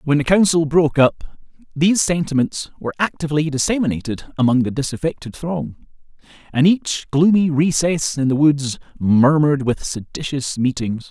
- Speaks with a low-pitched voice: No, medium, 145 Hz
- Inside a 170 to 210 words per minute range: No, slow, 135 wpm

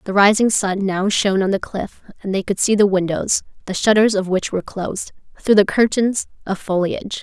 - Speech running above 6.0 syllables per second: No, 5.5 syllables/s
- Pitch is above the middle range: Yes, high, 200 Hz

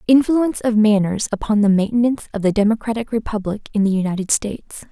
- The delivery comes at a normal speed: Yes, average, 170 wpm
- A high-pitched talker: Yes, high, 215 Hz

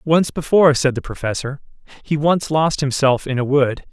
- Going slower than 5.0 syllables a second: No, 5.1 syllables/s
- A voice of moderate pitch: Yes, medium, 145 Hz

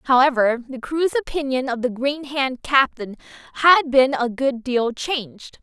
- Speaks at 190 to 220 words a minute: No, average, 160 wpm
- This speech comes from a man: No, female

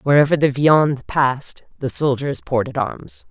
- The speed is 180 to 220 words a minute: No, average, 145 wpm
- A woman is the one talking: Yes, female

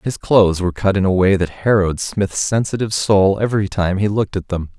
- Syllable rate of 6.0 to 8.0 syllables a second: Yes, 6.1 syllables/s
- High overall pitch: No, low, 100 Hz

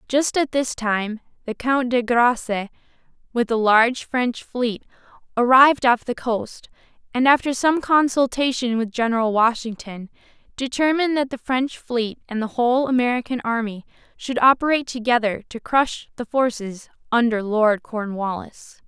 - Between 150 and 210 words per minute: No, average, 140 wpm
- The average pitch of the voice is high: Yes, high, 240 Hz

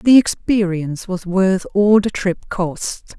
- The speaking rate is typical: Yes, average, 150 wpm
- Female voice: Yes, female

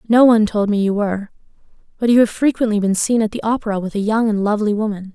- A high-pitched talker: Yes, high, 215 Hz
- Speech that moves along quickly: Yes, fast, 245 wpm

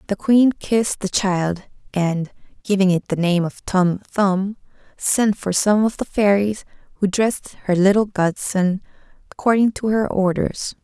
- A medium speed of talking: Yes, average, 155 wpm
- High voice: Yes, high, 195 Hz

